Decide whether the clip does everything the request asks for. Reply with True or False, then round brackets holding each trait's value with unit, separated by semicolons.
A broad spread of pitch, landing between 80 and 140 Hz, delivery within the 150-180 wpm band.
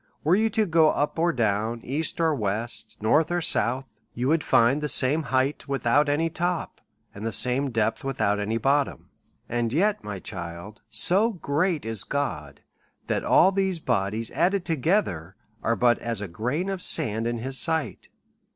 True (6.4 semitones; 135 Hz; 170 wpm)